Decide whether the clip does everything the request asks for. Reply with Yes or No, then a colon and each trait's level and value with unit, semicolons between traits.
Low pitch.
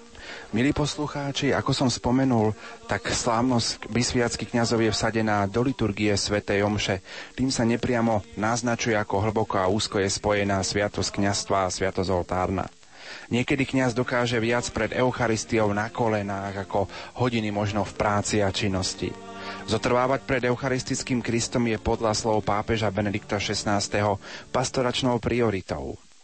Yes: low, 110 Hz